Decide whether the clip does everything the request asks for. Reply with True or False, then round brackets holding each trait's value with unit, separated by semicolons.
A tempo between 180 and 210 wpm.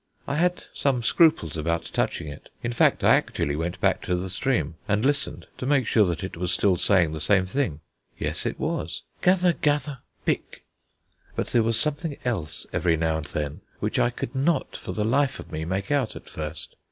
True (200 wpm)